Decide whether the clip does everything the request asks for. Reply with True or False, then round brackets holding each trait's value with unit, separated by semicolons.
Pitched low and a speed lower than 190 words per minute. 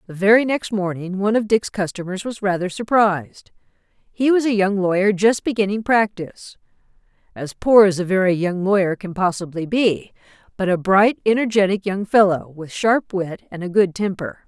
False (195 Hz; 170 wpm)